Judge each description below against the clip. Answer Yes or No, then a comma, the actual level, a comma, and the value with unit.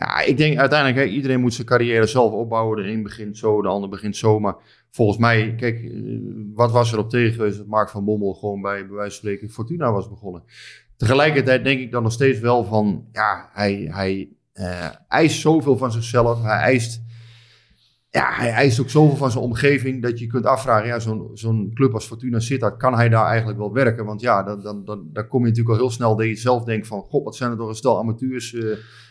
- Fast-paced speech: Yes, fast, 225 wpm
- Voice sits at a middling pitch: No, low, 115 Hz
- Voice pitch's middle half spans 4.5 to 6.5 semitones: No, average, 3.0 semitones